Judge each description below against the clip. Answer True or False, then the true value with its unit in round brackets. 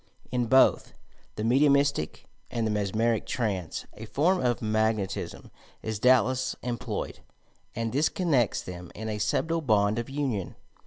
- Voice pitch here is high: False (115 Hz)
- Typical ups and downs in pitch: True (3.4 semitones)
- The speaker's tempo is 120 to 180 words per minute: True (140 wpm)